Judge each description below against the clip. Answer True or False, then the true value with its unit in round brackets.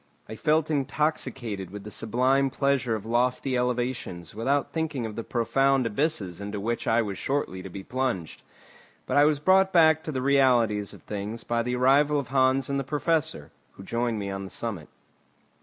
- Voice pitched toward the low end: True (125 Hz)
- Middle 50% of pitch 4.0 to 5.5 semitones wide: True (4.5 semitones)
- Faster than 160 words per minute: True (185 wpm)